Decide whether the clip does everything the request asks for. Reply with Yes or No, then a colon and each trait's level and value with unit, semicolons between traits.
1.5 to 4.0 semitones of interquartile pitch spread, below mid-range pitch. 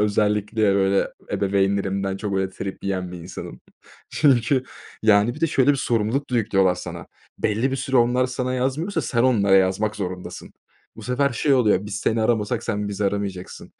No: average, 4.4 semitones; low, 105 Hz